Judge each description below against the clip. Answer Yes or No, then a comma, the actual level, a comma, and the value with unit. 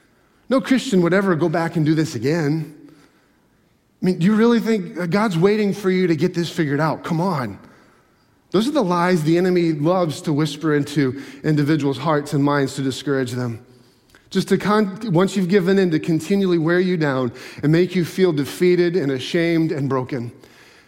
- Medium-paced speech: Yes, average, 185 wpm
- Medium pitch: Yes, medium, 170 Hz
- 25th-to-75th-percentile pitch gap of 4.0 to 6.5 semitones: Yes, average, 4.3 semitones